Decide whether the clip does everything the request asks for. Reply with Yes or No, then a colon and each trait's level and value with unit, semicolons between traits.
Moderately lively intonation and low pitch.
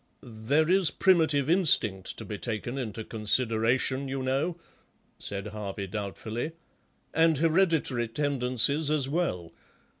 No: wide, 5.9 semitones; low, 130 Hz